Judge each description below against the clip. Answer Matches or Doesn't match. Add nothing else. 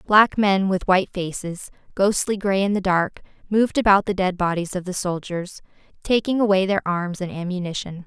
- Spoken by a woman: Matches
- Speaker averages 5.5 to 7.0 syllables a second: Doesn't match